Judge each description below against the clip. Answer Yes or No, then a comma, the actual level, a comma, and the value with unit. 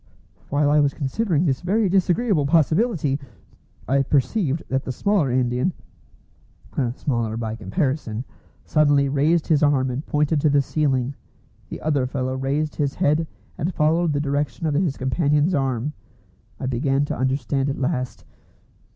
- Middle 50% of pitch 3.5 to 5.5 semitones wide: No, average, 2.9 semitones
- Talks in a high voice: No, medium, 145 Hz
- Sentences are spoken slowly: No, average, 145 wpm